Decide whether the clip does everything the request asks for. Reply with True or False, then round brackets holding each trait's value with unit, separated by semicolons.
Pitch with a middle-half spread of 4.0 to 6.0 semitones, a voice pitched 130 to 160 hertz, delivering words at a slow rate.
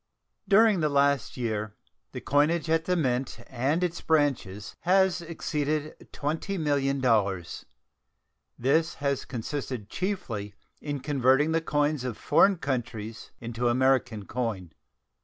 True (5.0 semitones; 140 Hz; 115 wpm)